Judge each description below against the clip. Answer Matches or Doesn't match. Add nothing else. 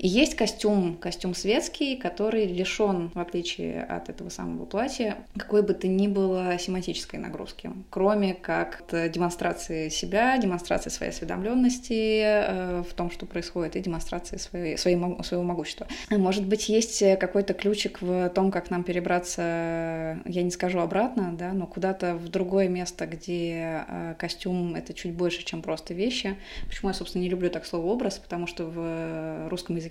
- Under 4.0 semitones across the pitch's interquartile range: Matches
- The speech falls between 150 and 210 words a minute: Matches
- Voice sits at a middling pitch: Matches